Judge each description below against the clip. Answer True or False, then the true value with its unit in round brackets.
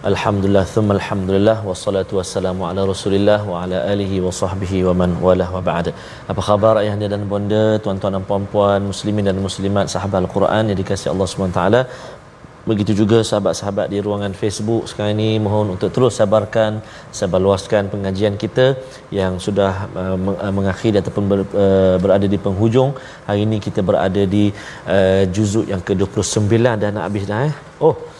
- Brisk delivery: True (165 wpm)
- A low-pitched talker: True (100 Hz)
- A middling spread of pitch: False (1.8 semitones)